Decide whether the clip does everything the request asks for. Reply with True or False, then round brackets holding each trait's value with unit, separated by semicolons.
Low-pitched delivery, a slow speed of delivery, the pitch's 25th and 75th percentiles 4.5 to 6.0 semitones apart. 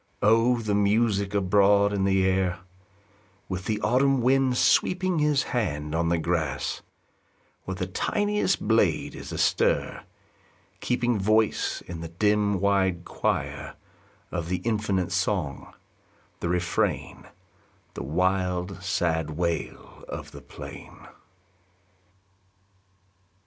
False (95 Hz; 110 wpm; 3.8 semitones)